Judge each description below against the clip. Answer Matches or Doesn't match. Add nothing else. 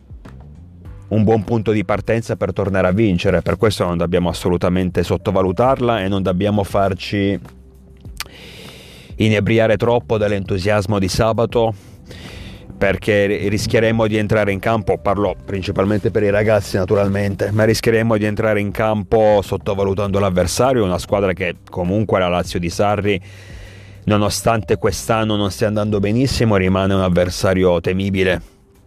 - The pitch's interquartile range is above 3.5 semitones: Doesn't match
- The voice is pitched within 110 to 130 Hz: Doesn't match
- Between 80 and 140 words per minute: Matches